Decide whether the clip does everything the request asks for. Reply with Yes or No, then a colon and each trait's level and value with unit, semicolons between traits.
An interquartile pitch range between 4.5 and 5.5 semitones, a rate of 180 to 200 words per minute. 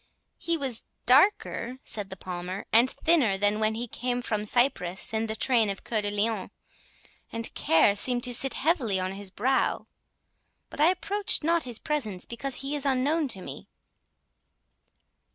No: average, 5.0 semitones; average, 165 wpm